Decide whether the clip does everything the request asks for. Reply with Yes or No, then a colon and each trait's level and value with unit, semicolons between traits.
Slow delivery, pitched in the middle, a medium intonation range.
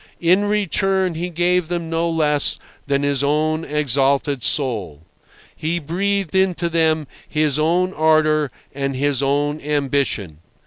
Yes: slow, 130 wpm; medium, 155 Hz; average, 3.3 semitones